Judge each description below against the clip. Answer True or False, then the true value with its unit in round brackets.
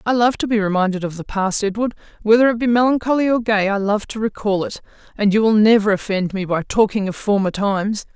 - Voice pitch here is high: True (210 Hz)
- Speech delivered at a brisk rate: True (215 wpm)